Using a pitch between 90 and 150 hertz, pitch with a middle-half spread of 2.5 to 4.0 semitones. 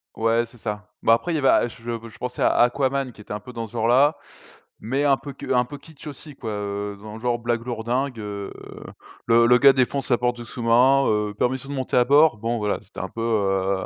Yes: low, 120 Hz; average, 3.3 semitones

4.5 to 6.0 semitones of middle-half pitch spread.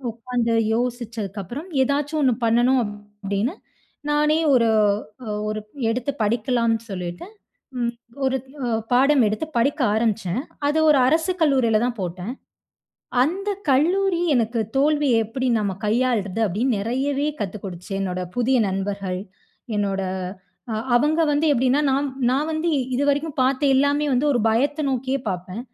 Yes: average, 5.2 semitones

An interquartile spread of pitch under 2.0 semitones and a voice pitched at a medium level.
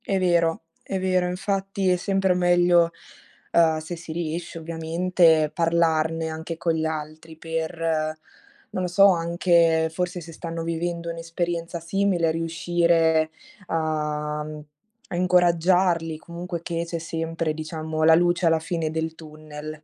Yes: narrow, 1.6 semitones; medium, 165 Hz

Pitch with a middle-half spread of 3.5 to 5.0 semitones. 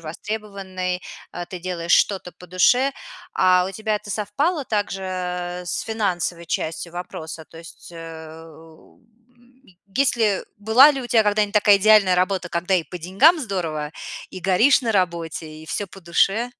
Yes: average, 3.8 semitones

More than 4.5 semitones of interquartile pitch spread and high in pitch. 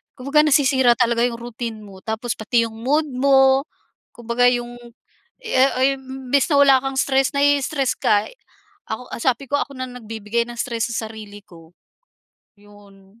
No: average, 3.2 semitones; high, 245 Hz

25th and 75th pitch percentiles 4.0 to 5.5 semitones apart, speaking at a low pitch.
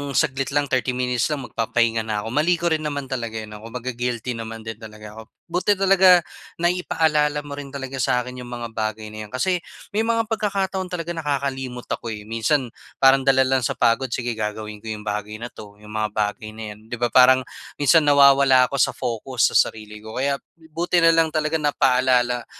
Yes: average, 4.8 semitones; low, 125 Hz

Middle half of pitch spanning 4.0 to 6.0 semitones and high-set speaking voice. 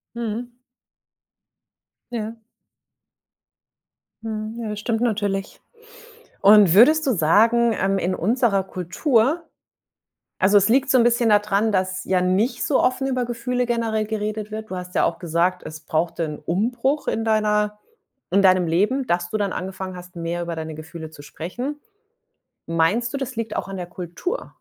Yes: average, 4.5 semitones; high, 210 Hz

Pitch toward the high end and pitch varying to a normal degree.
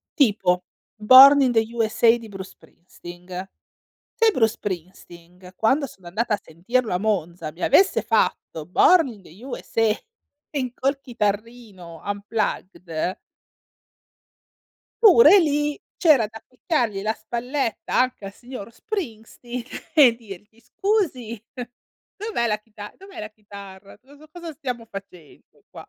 Yes: high, 225 Hz; average, 4.9 semitones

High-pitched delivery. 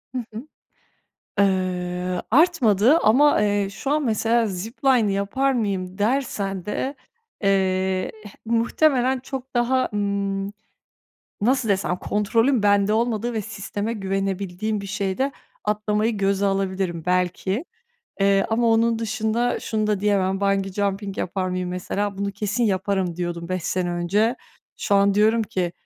Yes: high, 205 Hz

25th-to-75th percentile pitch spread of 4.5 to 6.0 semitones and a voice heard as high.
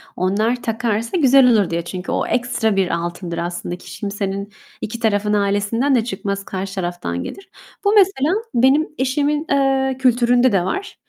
Yes: average, 5.3 semitones; high, 220 Hz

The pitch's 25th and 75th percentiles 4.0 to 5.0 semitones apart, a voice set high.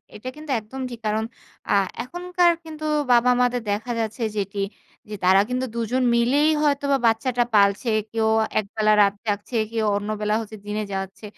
No: average, 3.4 semitones; high, 225 Hz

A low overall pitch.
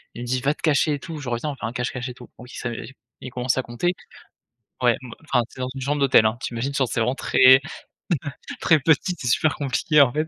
Yes: low, 130 Hz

